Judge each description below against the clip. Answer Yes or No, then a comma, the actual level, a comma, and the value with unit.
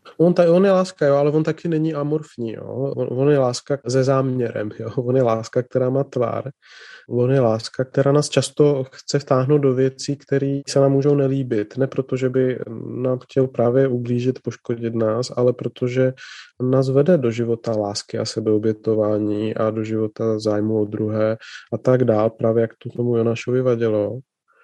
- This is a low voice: Yes, low, 130 Hz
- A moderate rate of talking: No, fast, 180 wpm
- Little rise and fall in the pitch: No, average, 3.1 semitones